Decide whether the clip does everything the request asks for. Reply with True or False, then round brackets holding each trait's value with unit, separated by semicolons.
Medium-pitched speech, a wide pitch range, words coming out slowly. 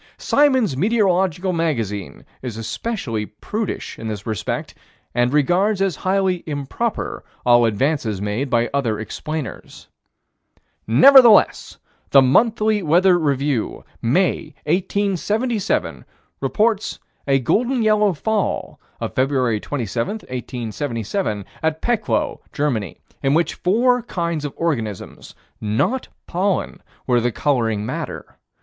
True (150 Hz; 9.0 semitones; 105 wpm)